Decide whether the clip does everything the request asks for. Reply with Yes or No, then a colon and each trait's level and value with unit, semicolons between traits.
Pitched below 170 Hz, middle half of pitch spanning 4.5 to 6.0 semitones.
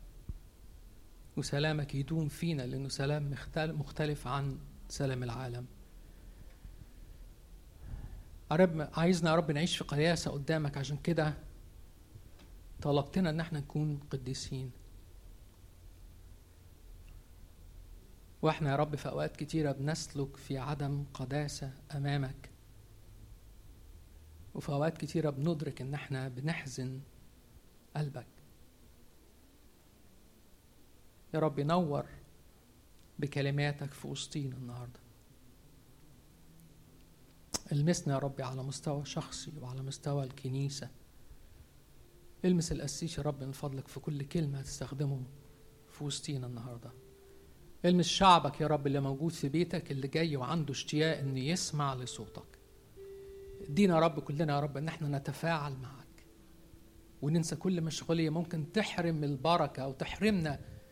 Yes: medium, 140 Hz; wide, 5.4 semitones